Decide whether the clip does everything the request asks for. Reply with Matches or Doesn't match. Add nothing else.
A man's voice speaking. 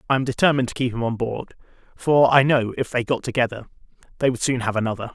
Matches